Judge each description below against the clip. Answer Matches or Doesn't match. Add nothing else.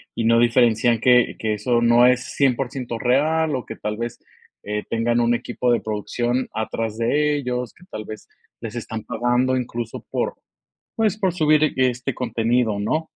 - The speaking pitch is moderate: Doesn't match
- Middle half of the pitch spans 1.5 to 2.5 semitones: Matches